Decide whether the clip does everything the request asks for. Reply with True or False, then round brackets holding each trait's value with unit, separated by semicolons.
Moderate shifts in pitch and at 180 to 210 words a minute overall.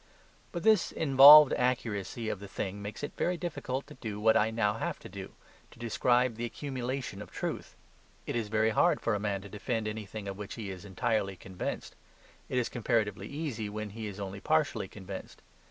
True (3.7 semitones; 195 wpm)